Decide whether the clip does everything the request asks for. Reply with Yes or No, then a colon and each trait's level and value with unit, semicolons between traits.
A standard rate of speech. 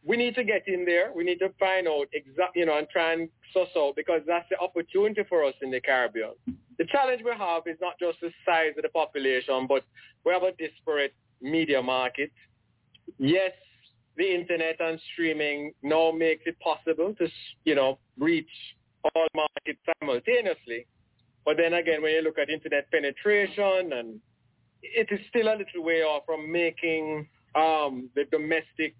Yes: average, 175 wpm